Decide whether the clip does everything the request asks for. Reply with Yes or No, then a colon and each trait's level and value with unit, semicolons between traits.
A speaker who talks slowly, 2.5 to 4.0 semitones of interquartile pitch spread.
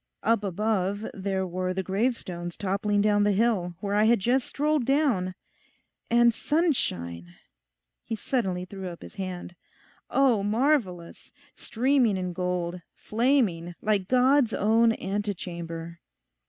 No: slow, 125 wpm; average, 4.6 semitones